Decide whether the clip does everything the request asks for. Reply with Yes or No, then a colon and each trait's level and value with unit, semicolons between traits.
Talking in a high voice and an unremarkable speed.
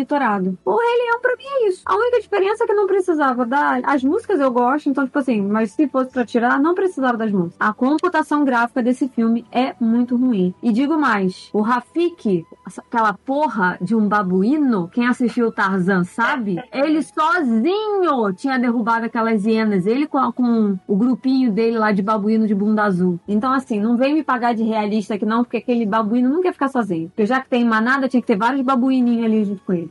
No: high, 245 Hz; fast, 210 wpm